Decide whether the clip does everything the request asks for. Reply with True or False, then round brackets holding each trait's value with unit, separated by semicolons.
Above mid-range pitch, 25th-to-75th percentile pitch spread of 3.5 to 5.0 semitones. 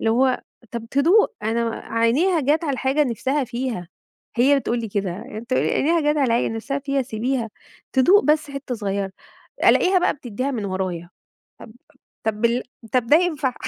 True (255 Hz; 4.1 semitones)